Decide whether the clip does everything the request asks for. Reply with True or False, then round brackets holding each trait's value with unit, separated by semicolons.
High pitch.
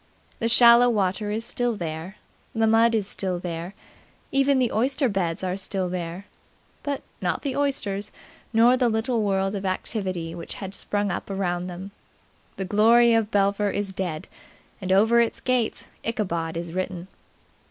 True (200 Hz)